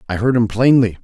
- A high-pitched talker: No, low, 115 Hz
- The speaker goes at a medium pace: No, fast, 230 wpm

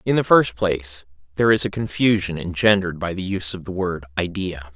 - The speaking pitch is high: No, very low, 90 Hz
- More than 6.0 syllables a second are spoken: No, 5.9 syllables/s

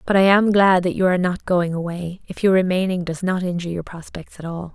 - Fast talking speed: Yes, fast, 240 wpm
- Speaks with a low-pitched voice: No, medium, 180 Hz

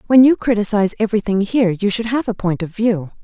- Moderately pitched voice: No, high, 215 Hz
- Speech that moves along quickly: Yes, fast, 225 wpm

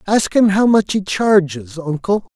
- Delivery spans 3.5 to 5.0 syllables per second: Yes, 4.1 syllables/s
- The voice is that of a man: Yes, male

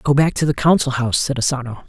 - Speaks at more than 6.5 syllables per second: Yes, 6.8 syllables/s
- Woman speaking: No, male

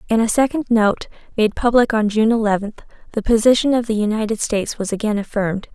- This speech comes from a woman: Yes, female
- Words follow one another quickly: No, average, 190 wpm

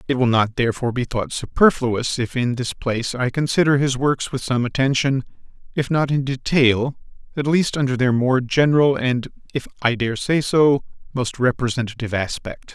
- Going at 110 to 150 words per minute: No, average, 175 wpm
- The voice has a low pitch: Yes, low, 130 Hz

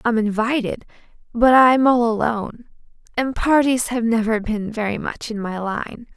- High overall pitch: Yes, high, 230 Hz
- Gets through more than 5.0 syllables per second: No, 4.5 syllables/s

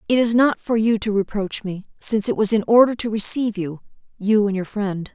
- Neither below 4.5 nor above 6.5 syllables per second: Yes, 5.5 syllables/s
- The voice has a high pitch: Yes, high, 210 Hz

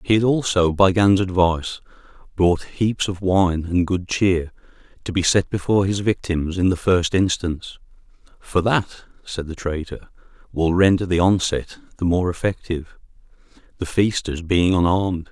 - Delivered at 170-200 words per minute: No, average, 155 wpm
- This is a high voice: No, very low, 90 Hz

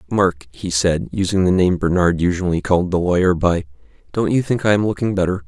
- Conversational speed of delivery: No, fast, 210 wpm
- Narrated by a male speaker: Yes, male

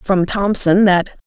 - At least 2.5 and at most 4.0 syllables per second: Yes, 3.9 syllables/s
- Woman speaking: Yes, female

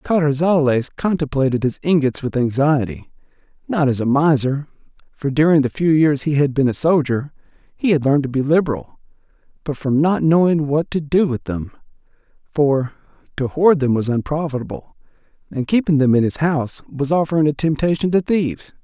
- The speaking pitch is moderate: Yes, medium, 145 Hz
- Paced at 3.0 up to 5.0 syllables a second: No, 5.4 syllables/s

